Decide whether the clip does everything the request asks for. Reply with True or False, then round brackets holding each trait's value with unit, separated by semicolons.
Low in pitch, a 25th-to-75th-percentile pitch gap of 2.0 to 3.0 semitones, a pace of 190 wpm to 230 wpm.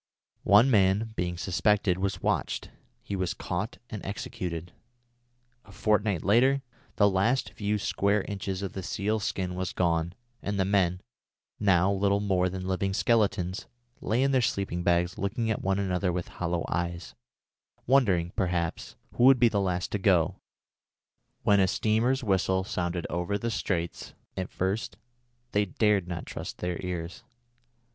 False (95 Hz; 2.6 semitones; 150 wpm)